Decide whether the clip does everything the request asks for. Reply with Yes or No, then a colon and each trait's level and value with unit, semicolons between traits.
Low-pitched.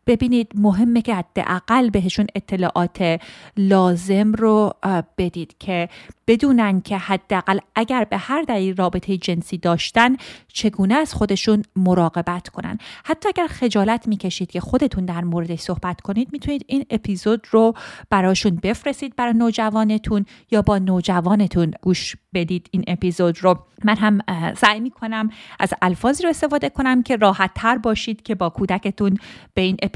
No: high, 200 Hz